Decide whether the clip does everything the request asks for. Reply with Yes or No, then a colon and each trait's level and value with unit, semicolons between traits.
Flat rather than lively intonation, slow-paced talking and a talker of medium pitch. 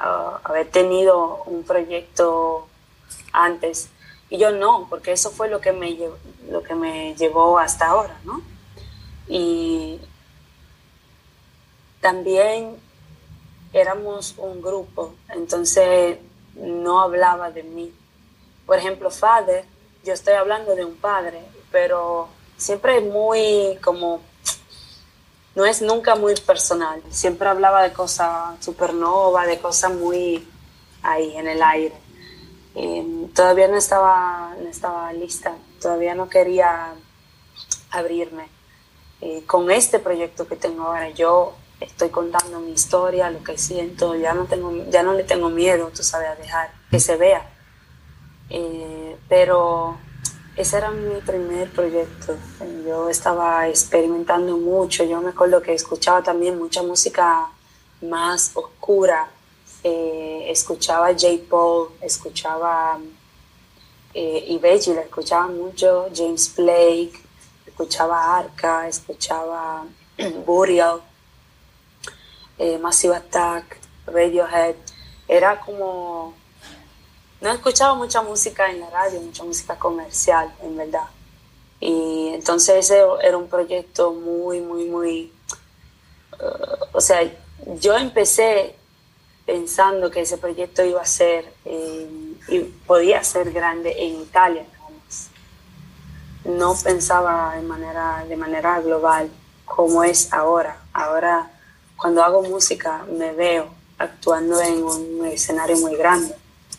Yes: narrow, 2.0 semitones; slow, 120 wpm; medium, 170 Hz